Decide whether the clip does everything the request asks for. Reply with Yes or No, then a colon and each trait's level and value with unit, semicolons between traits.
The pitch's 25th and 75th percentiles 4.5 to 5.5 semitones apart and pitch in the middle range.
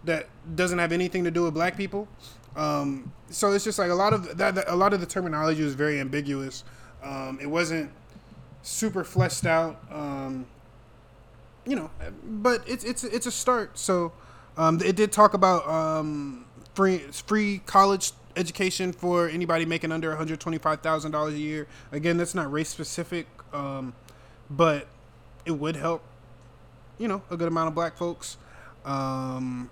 Yes: average, 4.8 semitones; medium, 160 Hz